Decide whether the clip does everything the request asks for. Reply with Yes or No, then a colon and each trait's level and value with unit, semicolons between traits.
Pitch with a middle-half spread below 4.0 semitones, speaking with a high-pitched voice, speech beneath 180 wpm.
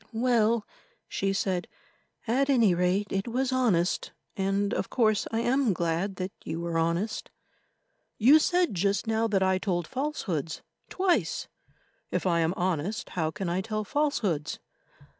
No: average, 4.8 semitones; high, 200 Hz; average, 140 wpm